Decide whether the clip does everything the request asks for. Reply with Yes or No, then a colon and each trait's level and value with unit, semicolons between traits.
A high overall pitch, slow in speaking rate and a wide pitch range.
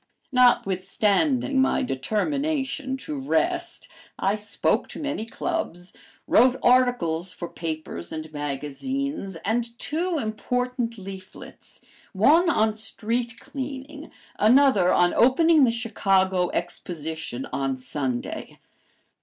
Yes: high, 230 Hz; slow, 100 wpm; wide, 7.1 semitones